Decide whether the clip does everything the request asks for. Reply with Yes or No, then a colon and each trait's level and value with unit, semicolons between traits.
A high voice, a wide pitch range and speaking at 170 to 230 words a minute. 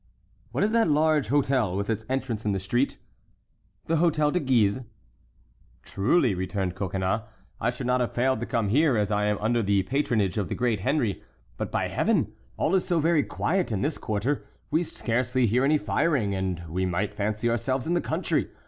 No: low, 120 Hz; wide, 6.0 semitones; average, 195 wpm